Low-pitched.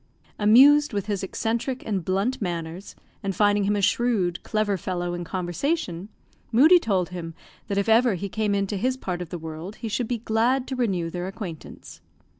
No: high, 200 Hz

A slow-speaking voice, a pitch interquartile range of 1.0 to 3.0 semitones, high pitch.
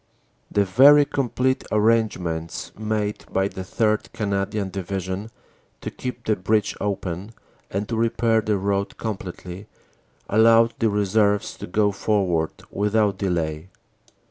No: slow, 125 wpm; average, 2.7 semitones; low, 105 Hz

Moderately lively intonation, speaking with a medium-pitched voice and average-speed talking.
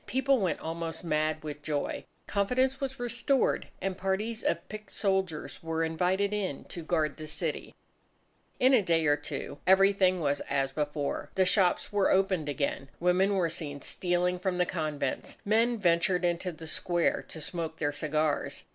Yes: average, 3.9 semitones; medium, 175 Hz; average, 165 wpm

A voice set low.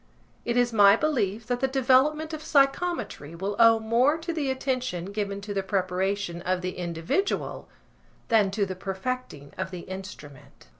No: high, 205 Hz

